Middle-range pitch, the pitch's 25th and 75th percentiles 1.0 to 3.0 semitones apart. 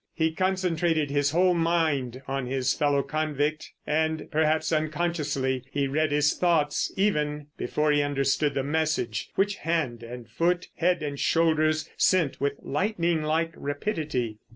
Yes: medium, 155 Hz; narrow, 2.6 semitones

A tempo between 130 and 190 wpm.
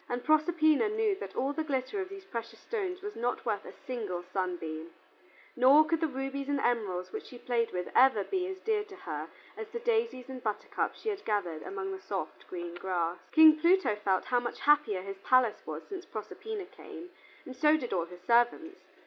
No: average, 200 wpm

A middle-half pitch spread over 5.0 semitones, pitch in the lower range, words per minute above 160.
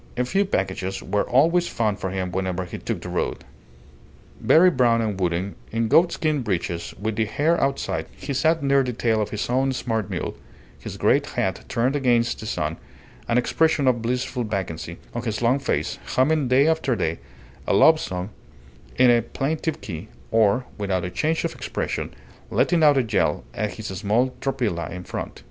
Yes: wide, 5.5 semitones; low, 120 Hz; average, 180 wpm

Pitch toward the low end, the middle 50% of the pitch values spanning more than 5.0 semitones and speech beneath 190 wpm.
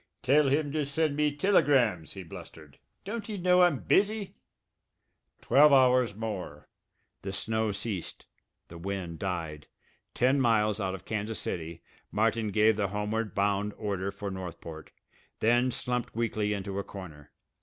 Yes: low, 105 Hz; wide, 5.5 semitones; average, 145 wpm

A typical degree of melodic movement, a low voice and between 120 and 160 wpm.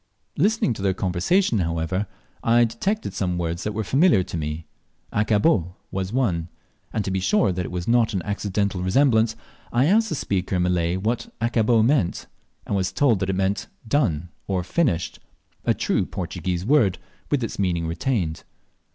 No: average, 4.9 semitones; low, 100 Hz; average, 170 wpm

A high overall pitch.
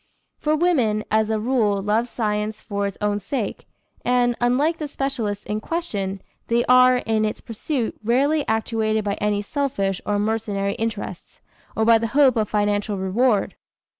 Yes: high, 220 Hz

